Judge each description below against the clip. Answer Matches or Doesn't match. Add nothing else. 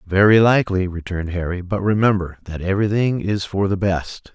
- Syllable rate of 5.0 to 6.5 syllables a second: Matches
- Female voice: Doesn't match